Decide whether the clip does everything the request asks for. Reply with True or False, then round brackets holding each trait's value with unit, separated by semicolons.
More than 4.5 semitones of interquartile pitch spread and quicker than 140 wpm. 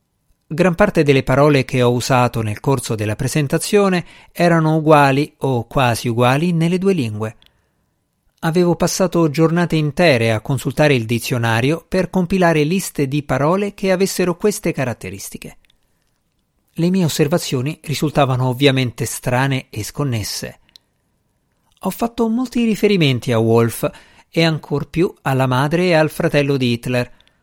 False (5.4 semitones; 130 wpm)